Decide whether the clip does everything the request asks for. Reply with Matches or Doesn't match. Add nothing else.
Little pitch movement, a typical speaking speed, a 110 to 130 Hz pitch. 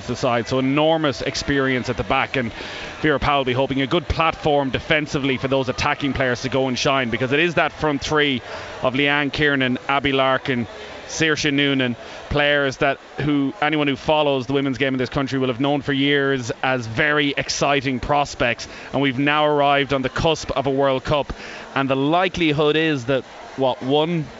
Doesn't match